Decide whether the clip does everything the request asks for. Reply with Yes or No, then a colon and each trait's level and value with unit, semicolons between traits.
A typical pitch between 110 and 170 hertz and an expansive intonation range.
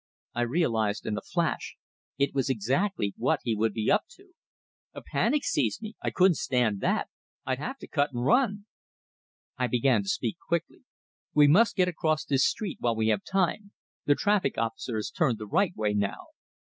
Yes: medium, 140 Hz; wide, 9.0 semitones